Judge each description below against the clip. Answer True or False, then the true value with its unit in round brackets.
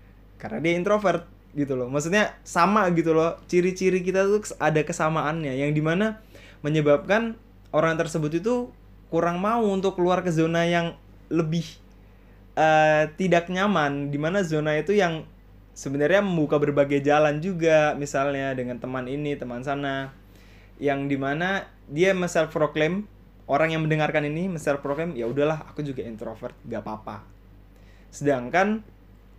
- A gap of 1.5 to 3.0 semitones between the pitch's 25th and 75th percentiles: False (4.2 semitones)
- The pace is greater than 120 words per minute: True (130 wpm)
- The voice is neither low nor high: True (155 Hz)